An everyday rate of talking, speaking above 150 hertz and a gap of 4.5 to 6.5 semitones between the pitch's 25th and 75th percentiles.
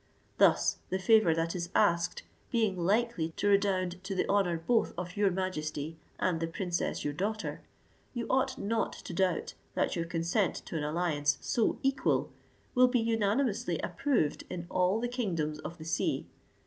Yes: average, 165 wpm; medium, 185 Hz; average, 4.9 semitones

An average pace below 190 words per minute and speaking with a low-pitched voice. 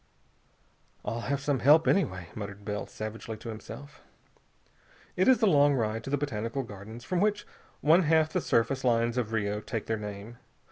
Yes: average, 175 wpm; low, 115 Hz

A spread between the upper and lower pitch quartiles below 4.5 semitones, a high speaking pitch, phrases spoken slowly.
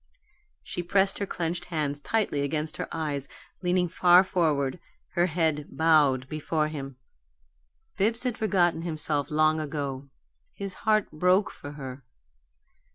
No: average, 3.8 semitones; medium, 160 Hz; slow, 130 wpm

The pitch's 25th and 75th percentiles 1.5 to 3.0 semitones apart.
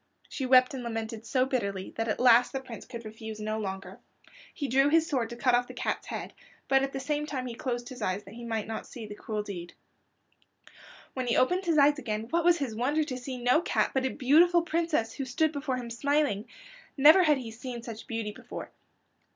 No: average, 4.1 semitones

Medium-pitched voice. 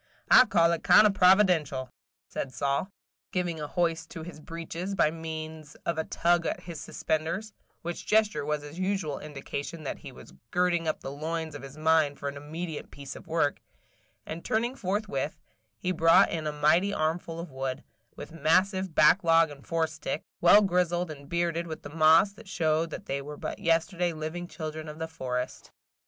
Yes: medium, 160 Hz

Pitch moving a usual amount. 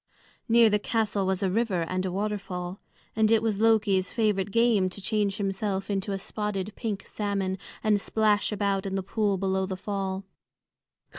No: narrow, 2.0 semitones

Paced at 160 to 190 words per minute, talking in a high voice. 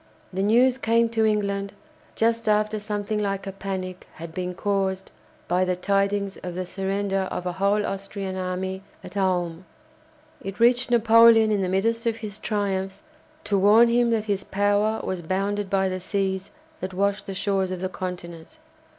Yes: average, 170 wpm; high, 195 Hz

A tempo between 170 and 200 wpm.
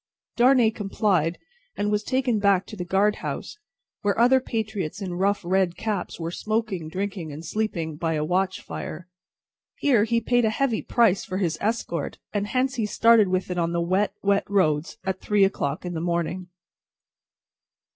Yes: average, 175 wpm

